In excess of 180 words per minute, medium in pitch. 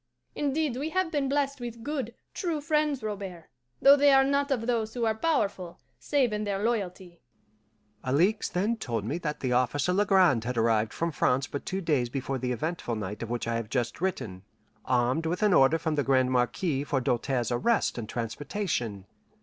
Yes: average, 190 wpm; medium, 175 Hz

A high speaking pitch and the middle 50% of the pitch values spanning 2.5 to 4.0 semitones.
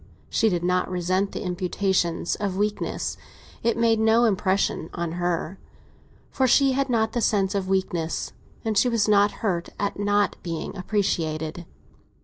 Yes: high, 195 Hz; average, 3.6 semitones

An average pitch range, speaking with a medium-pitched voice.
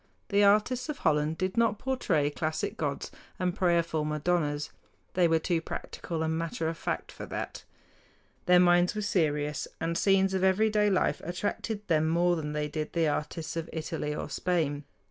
Yes: average, 3.4 semitones; medium, 170 Hz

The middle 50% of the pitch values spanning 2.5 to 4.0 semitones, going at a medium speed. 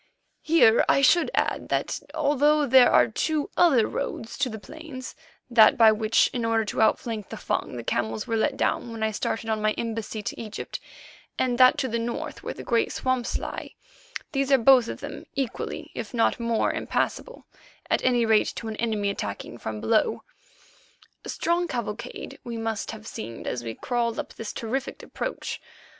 Yes: average, 3.3 semitones; average, 180 wpm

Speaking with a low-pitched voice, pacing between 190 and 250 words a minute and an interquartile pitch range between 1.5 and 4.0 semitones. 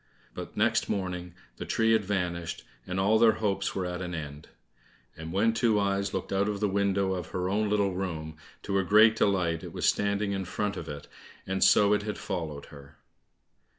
Yes: very low, 95 Hz; average, 200 wpm; narrow, 2.6 semitones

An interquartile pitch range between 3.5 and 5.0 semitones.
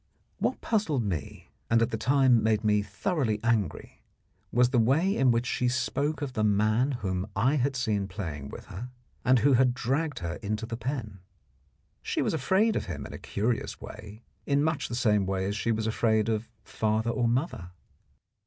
Yes: average, 3.9 semitones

